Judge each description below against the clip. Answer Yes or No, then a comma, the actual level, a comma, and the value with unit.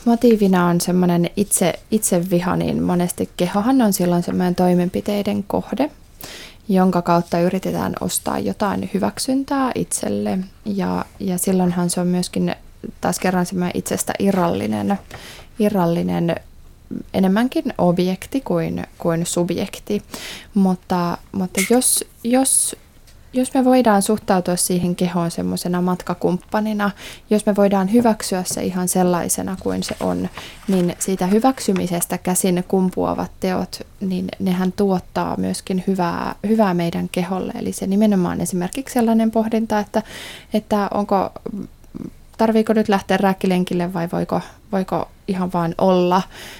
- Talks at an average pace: Yes, average, 120 wpm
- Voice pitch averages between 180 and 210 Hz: Yes, medium, 185 Hz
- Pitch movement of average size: Yes, average, 3.0 semitones